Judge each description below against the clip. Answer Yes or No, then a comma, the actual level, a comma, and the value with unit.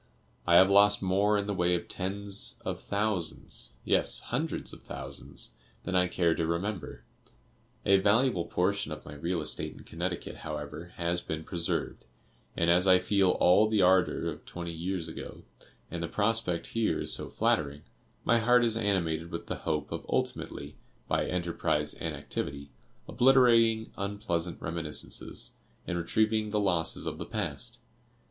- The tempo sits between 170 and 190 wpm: No, average, 155 wpm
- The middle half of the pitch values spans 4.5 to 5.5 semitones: No, average, 3.6 semitones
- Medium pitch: No, very low, 90 Hz